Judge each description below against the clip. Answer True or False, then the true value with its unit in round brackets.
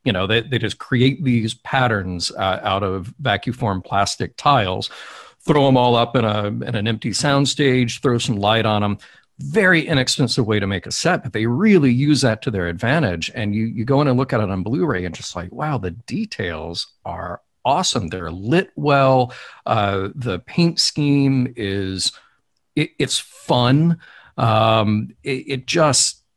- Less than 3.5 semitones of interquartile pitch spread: False (4.6 semitones)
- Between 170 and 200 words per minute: True (180 wpm)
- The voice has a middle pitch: False (120 Hz)